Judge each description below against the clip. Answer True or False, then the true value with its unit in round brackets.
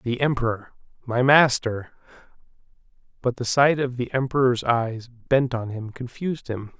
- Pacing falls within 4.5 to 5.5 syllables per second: True (4.6 syllables/s)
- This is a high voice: False (125 Hz)